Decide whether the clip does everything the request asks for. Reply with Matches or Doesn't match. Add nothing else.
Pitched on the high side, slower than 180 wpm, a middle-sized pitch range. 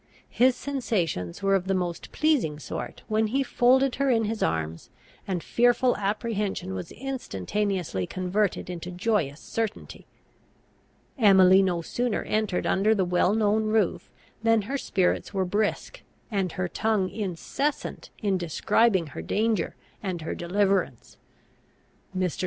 Matches